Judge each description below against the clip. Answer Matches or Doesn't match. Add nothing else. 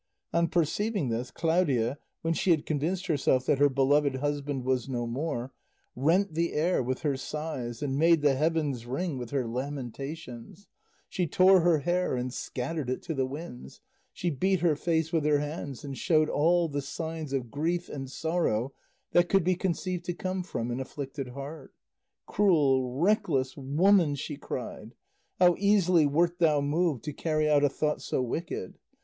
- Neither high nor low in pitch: Matches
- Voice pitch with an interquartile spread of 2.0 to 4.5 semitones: Matches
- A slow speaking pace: Doesn't match